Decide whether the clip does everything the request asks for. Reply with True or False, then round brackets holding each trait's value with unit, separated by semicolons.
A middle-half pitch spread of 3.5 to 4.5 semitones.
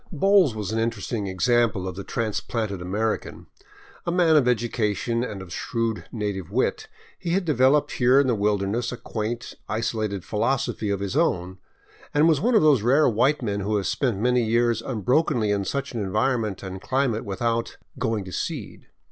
True (4.0 semitones)